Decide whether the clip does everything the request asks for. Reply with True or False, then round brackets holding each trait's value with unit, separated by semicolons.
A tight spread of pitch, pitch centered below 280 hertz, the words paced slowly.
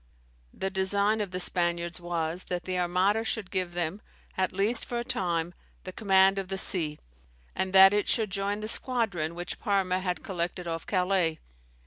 False (2.3 semitones; 185 Hz; 175 wpm)